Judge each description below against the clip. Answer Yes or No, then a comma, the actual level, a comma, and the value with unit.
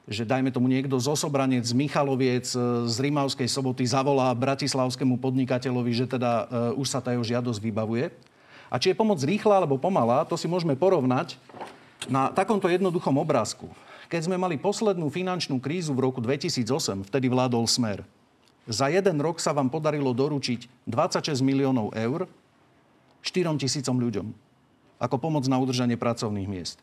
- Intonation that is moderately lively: Yes, average, 3.5 semitones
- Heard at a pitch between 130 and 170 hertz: Yes, low, 135 Hz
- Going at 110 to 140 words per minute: No, average, 160 wpm